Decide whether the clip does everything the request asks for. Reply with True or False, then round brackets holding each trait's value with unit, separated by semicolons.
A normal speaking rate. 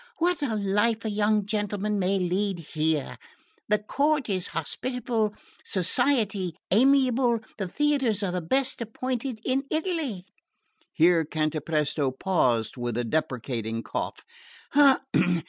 False (115 wpm)